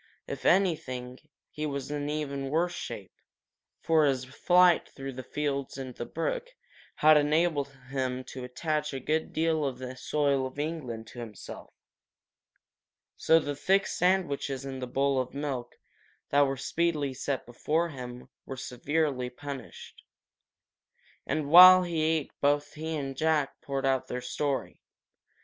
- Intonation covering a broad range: No, average, 3.2 semitones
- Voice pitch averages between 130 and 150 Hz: Yes, medium, 140 Hz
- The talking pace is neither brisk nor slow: Yes, average, 145 wpm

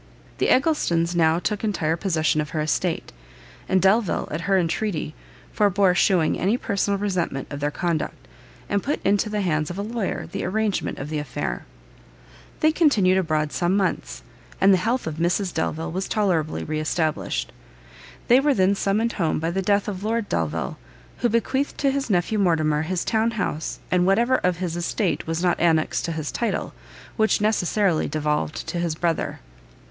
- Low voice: No, medium, 185 Hz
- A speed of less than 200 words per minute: Yes, average, 175 wpm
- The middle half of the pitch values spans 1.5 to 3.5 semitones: No, average, 4.6 semitones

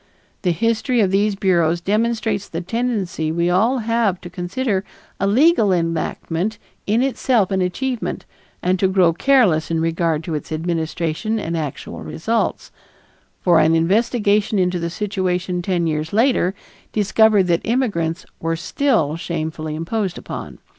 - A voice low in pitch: No, medium, 185 Hz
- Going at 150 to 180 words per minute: No, average, 140 wpm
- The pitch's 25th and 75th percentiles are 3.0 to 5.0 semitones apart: Yes, average, 4.7 semitones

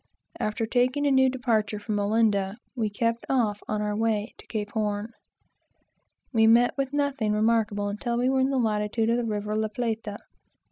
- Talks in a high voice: Yes, high, 220 Hz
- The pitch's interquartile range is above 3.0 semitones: No, narrow, 2.5 semitones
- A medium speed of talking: Yes, average, 180 wpm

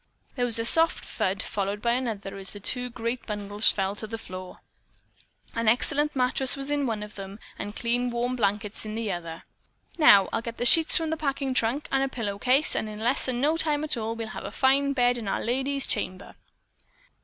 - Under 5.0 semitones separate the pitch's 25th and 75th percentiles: Yes, average, 4.3 semitones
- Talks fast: Yes, fast, 215 wpm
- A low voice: No, high, 235 Hz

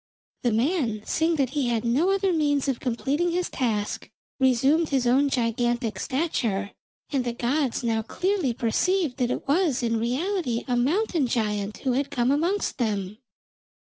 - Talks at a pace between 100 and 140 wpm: No, average, 160 wpm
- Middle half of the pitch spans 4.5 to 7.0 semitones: Yes, average, 5.0 semitones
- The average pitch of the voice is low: No, very high, 255 Hz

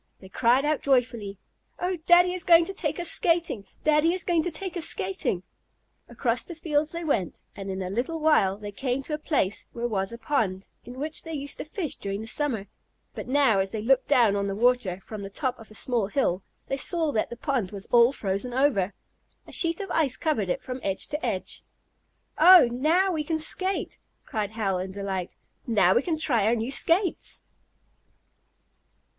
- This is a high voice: Yes, very high, 255 Hz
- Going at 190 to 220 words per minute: Yes, average, 200 wpm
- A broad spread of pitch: Yes, wide, 7.6 semitones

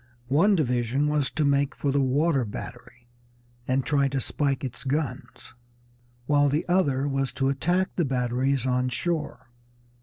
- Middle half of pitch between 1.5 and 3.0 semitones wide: Yes, narrow, 2.5 semitones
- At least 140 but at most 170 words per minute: Yes, average, 150 wpm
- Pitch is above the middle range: No, medium, 140 Hz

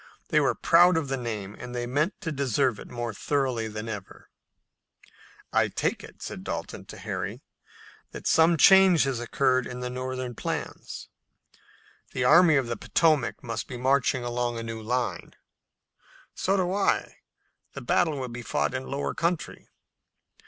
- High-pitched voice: No, low, 130 Hz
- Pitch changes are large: No, average, 4.2 semitones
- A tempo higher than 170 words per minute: No, average, 165 wpm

